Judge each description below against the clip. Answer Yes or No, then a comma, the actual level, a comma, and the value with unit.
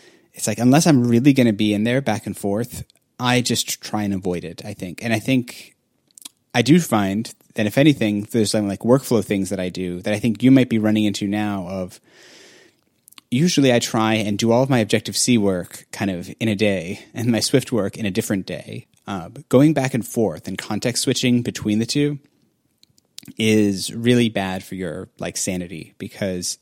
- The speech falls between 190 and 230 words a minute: Yes, fast, 205 wpm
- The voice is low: Yes, low, 110 Hz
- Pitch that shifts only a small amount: No, average, 3.5 semitones